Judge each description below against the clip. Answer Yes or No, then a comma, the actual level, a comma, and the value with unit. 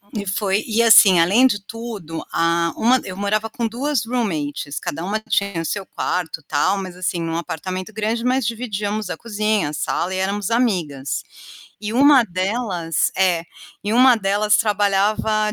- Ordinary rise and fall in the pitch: Yes, average, 3.6 semitones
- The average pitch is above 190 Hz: Yes, high, 205 Hz